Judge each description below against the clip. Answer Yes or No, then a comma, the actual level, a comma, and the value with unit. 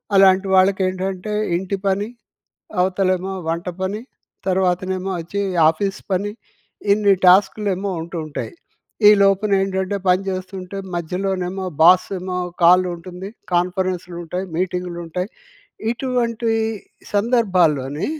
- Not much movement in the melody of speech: Yes, narrow, 1.6 semitones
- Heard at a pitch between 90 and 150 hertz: No, medium, 185 Hz